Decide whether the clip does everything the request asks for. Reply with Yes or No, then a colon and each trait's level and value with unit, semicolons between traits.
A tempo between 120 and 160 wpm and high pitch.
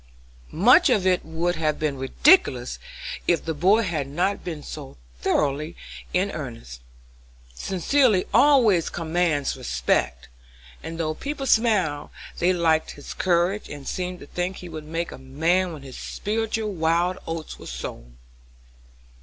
No: average, 140 wpm; medium, 170 Hz